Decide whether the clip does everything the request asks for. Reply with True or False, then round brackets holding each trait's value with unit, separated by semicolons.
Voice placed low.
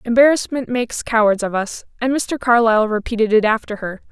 False (230 Hz)